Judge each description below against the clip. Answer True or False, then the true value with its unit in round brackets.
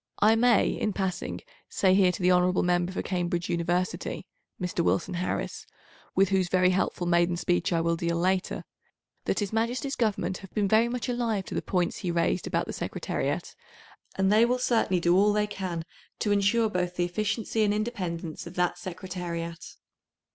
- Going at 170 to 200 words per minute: True (180 wpm)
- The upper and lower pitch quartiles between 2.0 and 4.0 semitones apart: True (3.1 semitones)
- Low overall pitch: False (185 Hz)